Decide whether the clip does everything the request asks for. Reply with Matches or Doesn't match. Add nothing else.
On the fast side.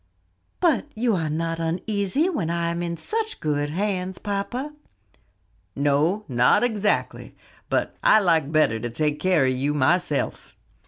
Doesn't match